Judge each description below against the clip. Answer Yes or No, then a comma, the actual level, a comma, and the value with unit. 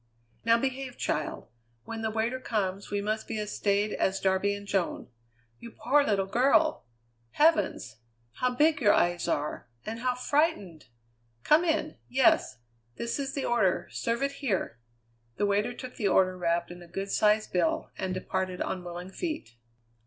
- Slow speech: No, average, 165 wpm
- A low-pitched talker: No, high, 210 Hz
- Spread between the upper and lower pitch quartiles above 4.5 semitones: Yes, average, 5.3 semitones